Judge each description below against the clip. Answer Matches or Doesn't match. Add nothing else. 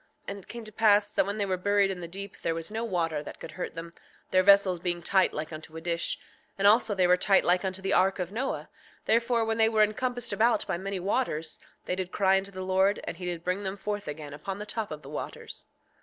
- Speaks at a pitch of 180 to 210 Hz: Matches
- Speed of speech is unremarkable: Doesn't match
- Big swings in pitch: Doesn't match